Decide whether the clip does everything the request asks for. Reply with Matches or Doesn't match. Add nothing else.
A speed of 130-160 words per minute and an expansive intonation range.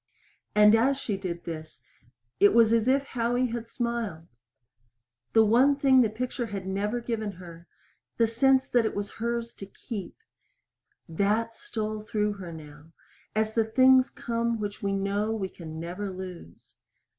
Doesn't match